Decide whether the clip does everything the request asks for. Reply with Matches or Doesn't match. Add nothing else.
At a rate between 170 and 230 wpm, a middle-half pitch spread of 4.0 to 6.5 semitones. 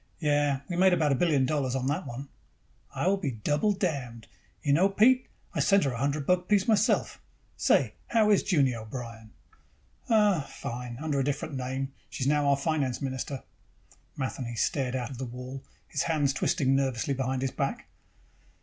Matches